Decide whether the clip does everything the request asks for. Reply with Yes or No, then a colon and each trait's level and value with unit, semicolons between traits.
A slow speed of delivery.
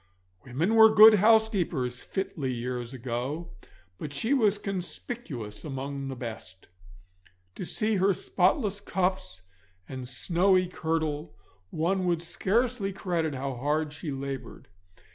Yes: slow, 120 wpm